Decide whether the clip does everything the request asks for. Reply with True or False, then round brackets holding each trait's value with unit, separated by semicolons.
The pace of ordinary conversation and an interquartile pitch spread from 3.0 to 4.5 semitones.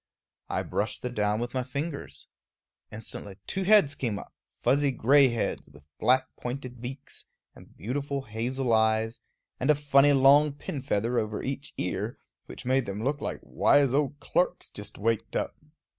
True (165 wpm; 4.1 semitones)